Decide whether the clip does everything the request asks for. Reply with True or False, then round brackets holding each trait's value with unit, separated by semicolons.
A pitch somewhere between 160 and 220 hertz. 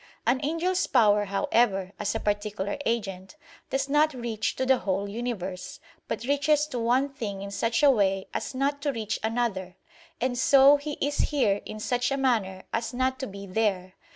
False (235 Hz)